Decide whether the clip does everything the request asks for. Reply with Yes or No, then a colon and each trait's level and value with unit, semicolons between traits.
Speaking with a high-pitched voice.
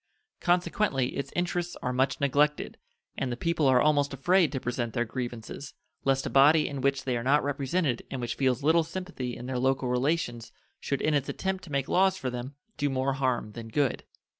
No: low, 135 Hz